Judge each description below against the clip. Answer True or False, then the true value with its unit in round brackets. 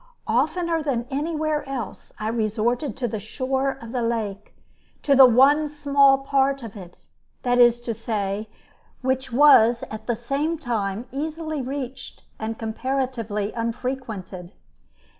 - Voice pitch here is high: True (250 Hz)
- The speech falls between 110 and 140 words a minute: True (135 wpm)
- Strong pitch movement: False (3.8 semitones)